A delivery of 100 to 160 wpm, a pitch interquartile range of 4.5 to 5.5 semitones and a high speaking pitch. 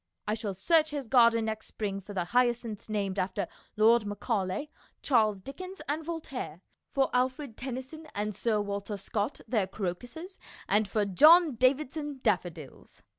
Yes: average, 145 wpm; average, 5.2 semitones; high, 225 Hz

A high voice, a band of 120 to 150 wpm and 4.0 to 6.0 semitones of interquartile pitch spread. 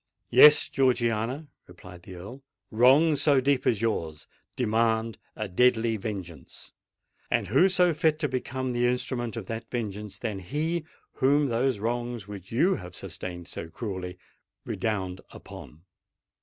No: low, 115 Hz; average, 140 wpm; average, 4.8 semitones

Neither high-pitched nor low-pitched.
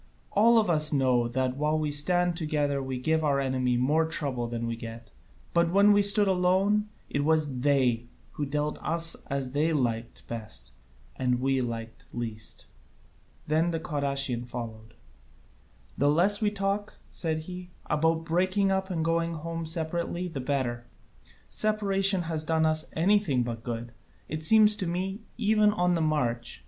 Yes: medium, 155 Hz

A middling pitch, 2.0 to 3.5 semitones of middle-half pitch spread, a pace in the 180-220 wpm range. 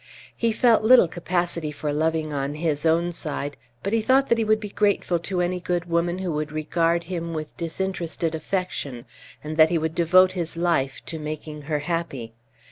Yes: medium, 170 Hz; average, 2.8 semitones; average, 190 wpm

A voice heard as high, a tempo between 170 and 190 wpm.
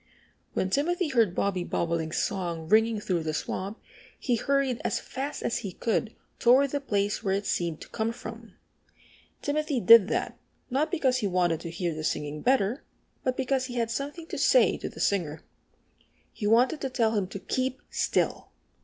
Yes: high, 225 Hz; average, 180 wpm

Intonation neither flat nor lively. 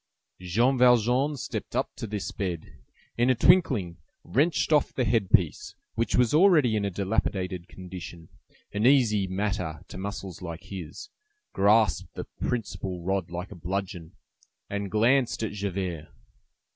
Yes: average, 4.7 semitones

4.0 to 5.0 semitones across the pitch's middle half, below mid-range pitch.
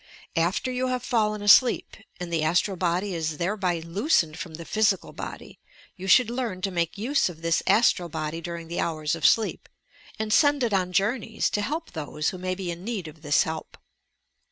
No: average, 4.6 semitones; medium, 185 Hz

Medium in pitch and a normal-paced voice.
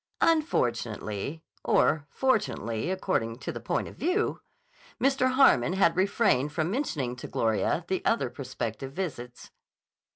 No: medium, 155 Hz; slow, 125 wpm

